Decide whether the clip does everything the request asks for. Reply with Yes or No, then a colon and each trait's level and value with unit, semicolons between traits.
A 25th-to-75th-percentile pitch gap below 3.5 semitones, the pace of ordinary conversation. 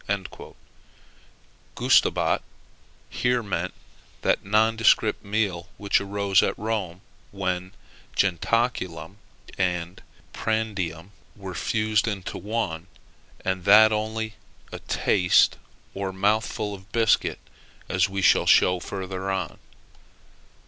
No: average, 2.8 semitones; slow, 95 wpm